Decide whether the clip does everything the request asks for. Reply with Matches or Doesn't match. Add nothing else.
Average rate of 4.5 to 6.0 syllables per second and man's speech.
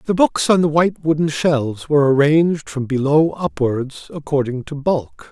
Matches